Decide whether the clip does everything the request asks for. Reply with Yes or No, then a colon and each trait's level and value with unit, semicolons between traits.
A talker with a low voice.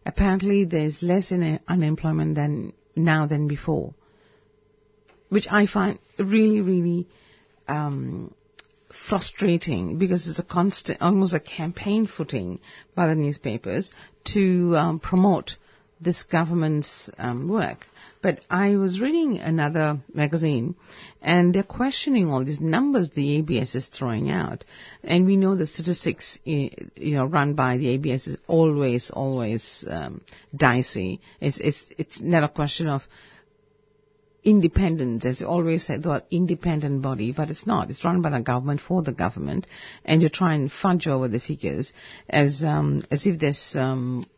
No: medium, 160 Hz